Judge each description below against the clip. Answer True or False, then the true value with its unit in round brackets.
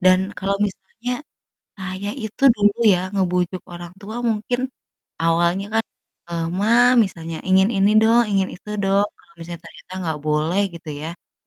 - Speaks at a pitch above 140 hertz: True (190 Hz)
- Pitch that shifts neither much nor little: True (3.0 semitones)